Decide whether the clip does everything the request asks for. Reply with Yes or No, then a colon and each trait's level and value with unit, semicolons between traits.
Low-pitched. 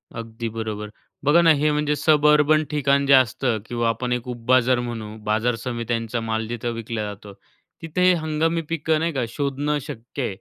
Yes: low, 125 Hz